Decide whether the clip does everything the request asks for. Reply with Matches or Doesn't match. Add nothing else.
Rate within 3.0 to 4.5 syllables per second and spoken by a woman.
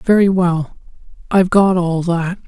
Doesn't match